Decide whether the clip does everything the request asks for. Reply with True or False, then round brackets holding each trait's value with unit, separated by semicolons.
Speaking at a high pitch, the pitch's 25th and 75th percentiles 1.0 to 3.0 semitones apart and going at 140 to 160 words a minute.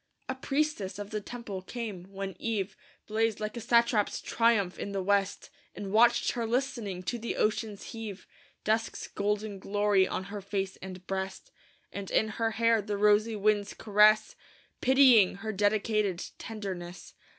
True (210 Hz; 2.5 semitones; 150 wpm)